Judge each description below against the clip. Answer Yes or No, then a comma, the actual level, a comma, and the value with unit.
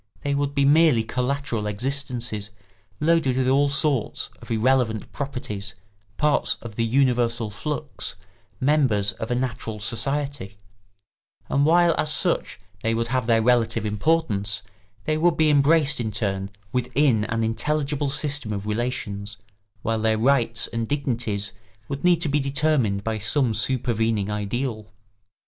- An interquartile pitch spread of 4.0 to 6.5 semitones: Yes, average, 4.5 semitones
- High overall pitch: No, low, 125 Hz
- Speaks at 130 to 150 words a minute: Yes, average, 140 wpm